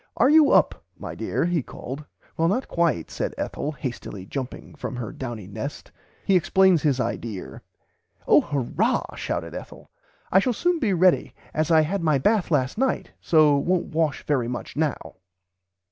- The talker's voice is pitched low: No, medium, 155 Hz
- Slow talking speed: No, average, 165 wpm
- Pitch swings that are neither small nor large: No, wide, 5.8 semitones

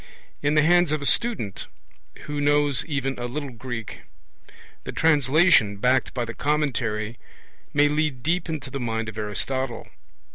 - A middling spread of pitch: Yes, average, 4.3 semitones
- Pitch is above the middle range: No, low, 135 Hz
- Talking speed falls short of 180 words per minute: Yes, average, 150 wpm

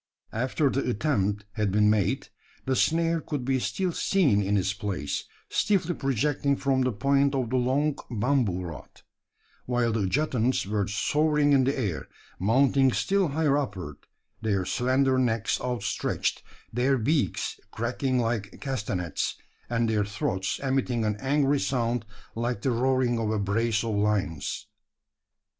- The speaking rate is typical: Yes, average, 145 wpm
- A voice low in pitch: Yes, low, 125 Hz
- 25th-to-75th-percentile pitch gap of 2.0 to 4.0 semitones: No, average, 4.7 semitones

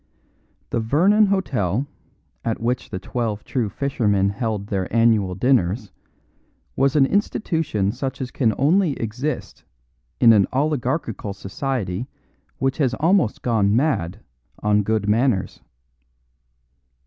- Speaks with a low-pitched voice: Yes, low, 115 Hz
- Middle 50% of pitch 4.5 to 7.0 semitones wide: Yes, average, 4.9 semitones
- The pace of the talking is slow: Yes, slow, 115 wpm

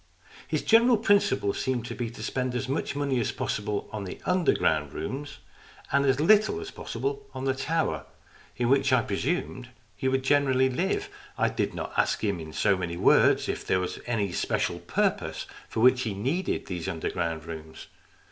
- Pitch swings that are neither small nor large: No, wide, 6.5 semitones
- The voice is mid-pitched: No, low, 130 Hz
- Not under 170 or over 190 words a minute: Yes, average, 185 wpm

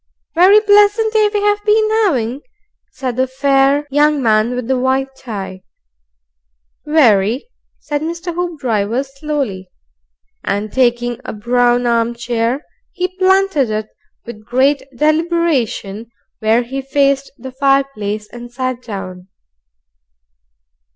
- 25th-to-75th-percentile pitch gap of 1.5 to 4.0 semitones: No, average, 4.7 semitones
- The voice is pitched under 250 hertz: No, very high, 260 Hz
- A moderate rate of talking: No, slow, 110 wpm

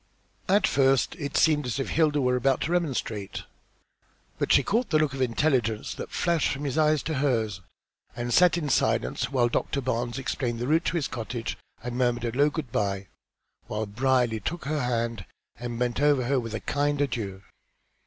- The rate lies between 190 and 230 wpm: Yes, average, 195 wpm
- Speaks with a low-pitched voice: Yes, low, 130 Hz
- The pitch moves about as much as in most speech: Yes, average, 3.8 semitones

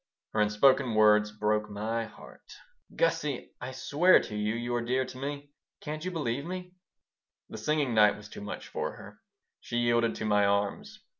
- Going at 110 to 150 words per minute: No, average, 170 wpm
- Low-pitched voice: Yes, low, 120 Hz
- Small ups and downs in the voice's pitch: No, average, 4.9 semitones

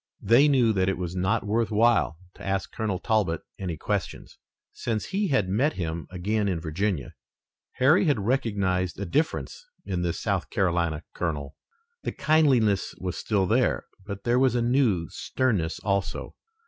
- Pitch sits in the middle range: No, low, 100 Hz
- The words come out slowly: No, average, 160 wpm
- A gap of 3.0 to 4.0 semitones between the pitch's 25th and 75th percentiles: No, average, 4.9 semitones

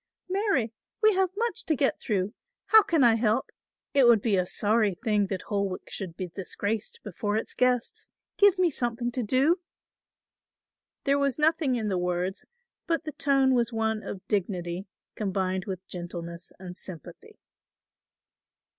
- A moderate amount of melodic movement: No, wide, 6.2 semitones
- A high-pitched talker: Yes, high, 220 Hz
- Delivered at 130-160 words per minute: Yes, average, 155 wpm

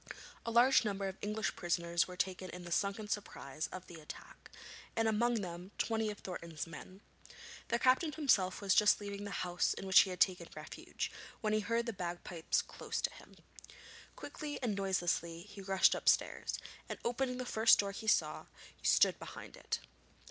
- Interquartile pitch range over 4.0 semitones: No, average, 3.7 semitones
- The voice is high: Yes, high, 200 Hz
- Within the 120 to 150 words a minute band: No, average, 175 wpm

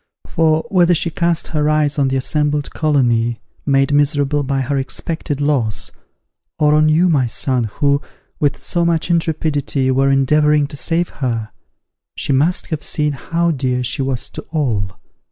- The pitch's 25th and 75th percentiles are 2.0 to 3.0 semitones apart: Yes, average, 2.7 semitones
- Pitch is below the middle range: No, medium, 145 Hz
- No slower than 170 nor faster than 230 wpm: No, average, 160 wpm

